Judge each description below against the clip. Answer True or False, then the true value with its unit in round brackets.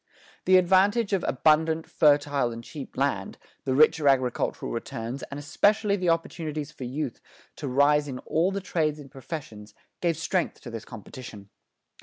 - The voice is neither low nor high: True (150 Hz)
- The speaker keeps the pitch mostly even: False (4.4 semitones)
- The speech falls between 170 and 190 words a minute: False (155 wpm)